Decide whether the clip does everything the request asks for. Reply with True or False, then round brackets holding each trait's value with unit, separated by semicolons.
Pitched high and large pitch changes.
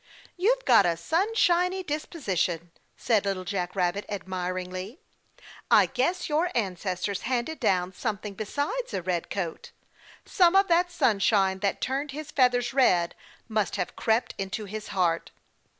True (215 Hz; 8.3 semitones)